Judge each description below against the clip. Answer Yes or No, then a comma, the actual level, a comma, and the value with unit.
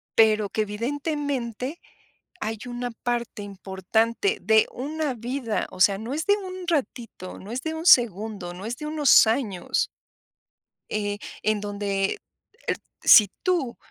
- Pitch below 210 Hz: No, high, 230 Hz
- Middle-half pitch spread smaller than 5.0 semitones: No, wide, 5.6 semitones